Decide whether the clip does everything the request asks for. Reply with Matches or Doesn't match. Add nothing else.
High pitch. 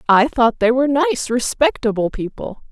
Matches